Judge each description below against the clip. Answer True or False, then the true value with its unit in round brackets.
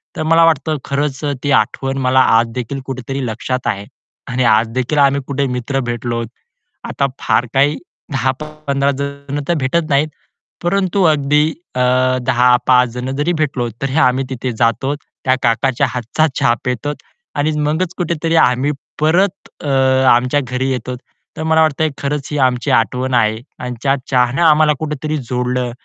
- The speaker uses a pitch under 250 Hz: True (135 Hz)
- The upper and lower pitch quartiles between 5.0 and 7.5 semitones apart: False (3.2 semitones)